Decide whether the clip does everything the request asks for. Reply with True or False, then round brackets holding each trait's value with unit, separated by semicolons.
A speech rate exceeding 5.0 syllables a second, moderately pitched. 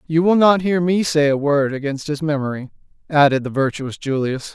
True (5.2 syllables/s; 150 Hz)